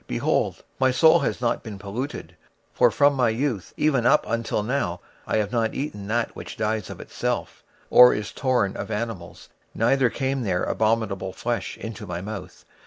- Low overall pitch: Yes, low, 115 Hz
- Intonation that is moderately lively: Yes, average, 3.8 semitones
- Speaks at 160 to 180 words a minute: Yes, average, 175 wpm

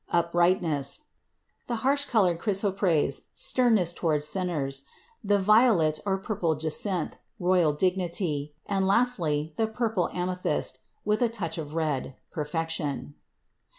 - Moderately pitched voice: Yes, medium, 175 Hz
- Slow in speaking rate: Yes, slow, 115 wpm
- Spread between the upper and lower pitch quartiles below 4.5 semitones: No, average, 4.8 semitones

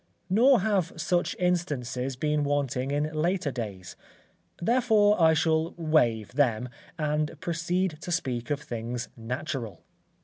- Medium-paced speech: No, slow, 125 wpm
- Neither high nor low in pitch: Yes, medium, 150 Hz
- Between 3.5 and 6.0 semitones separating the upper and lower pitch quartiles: Yes, wide, 5.6 semitones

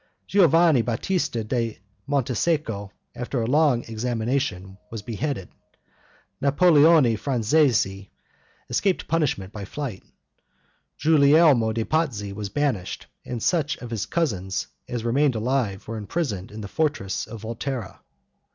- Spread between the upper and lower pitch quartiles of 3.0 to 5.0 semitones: No, wide, 5.6 semitones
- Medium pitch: No, low, 120 Hz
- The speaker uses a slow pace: Yes, slow, 115 wpm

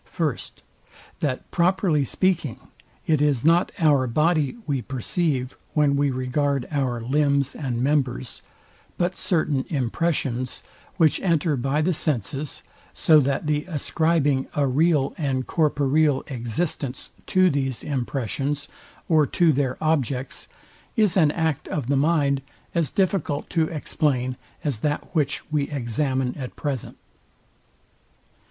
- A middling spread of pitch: Yes, average, 3.1 semitones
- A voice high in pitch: No, medium, 145 Hz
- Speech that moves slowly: Yes, slow, 125 wpm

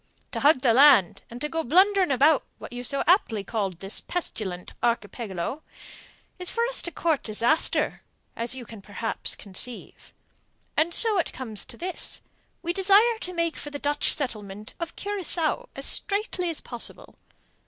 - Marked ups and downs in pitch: Yes, wide, 7.8 semitones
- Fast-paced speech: No, average, 160 wpm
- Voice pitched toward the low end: No, very high, 285 Hz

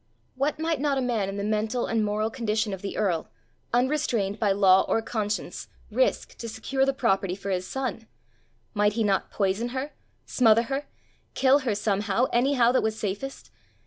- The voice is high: Yes, high, 225 Hz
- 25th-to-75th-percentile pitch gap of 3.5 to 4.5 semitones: Yes, average, 4.2 semitones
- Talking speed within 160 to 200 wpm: Yes, average, 175 wpm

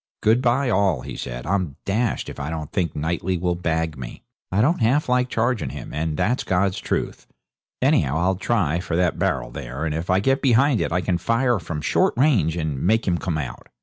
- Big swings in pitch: Yes, wide, 6.4 semitones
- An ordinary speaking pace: No, fast, 215 wpm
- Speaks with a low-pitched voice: Yes, very low, 90 Hz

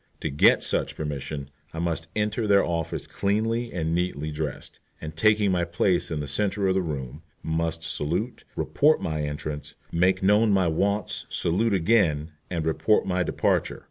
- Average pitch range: Yes, average, 4.4 semitones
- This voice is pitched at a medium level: No, very low, 85 Hz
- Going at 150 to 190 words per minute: Yes, average, 165 wpm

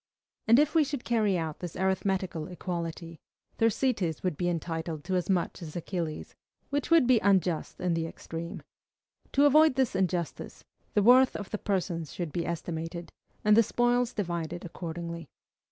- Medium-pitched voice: Yes, medium, 180 Hz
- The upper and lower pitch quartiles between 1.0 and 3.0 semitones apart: No, average, 5.0 semitones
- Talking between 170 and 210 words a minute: No, average, 160 wpm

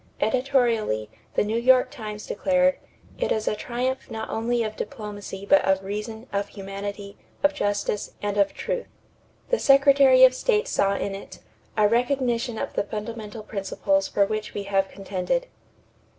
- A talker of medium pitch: No, high, 220 Hz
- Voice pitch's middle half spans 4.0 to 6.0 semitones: Yes, average, 4.3 semitones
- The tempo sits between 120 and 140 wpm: No, average, 155 wpm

